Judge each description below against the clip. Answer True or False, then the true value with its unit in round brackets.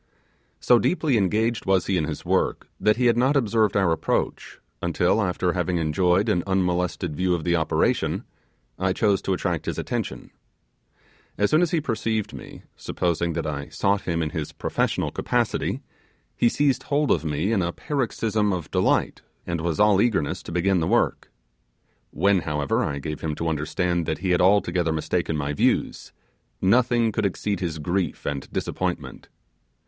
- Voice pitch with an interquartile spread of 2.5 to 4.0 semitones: False (4.4 semitones)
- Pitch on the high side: False (90 Hz)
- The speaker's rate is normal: True (170 wpm)